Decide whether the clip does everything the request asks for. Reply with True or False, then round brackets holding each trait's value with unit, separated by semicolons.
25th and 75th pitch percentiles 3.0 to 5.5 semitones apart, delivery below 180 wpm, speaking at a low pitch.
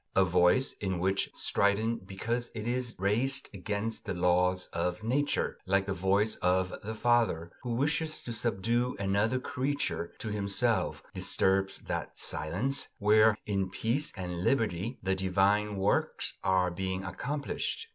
True (3.9 semitones; 140 wpm; 100 Hz)